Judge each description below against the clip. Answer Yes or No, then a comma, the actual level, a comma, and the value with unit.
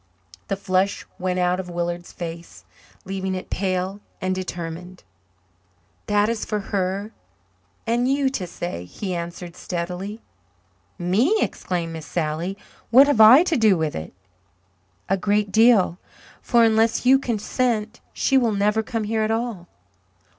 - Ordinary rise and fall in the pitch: Yes, average, 4.0 semitones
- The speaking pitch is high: Yes, high, 195 Hz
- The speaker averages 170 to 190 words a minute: No, average, 140 wpm